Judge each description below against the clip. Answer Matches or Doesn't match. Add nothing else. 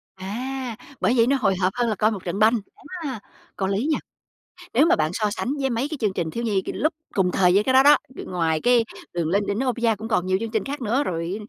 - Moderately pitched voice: Doesn't match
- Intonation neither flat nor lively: Matches